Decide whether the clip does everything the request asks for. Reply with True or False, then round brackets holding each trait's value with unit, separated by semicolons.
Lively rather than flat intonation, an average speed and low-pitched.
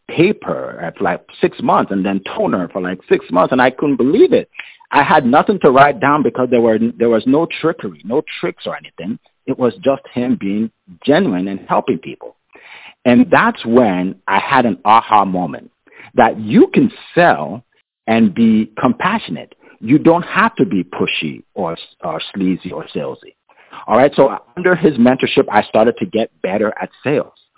True (6.2 semitones; 180 wpm; 115 Hz)